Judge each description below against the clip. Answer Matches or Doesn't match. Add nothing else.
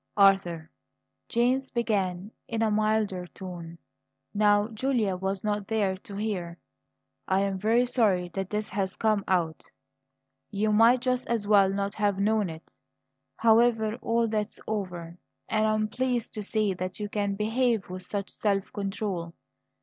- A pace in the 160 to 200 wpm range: Doesn't match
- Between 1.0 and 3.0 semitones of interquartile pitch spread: Matches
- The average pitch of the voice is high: Matches